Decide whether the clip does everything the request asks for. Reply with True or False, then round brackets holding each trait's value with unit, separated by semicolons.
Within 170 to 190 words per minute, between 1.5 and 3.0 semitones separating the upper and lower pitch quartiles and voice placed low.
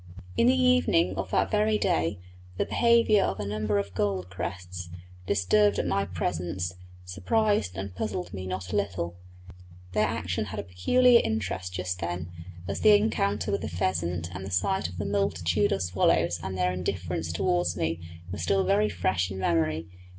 True (175 wpm; 2.5 semitones; 95 Hz)